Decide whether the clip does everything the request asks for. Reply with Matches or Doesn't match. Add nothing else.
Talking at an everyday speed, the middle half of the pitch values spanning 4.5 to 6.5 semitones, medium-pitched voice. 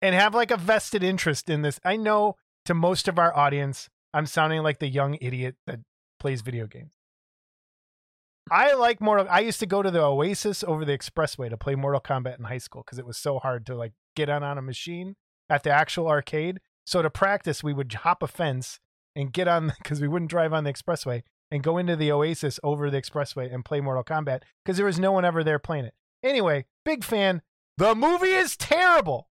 Doesn't match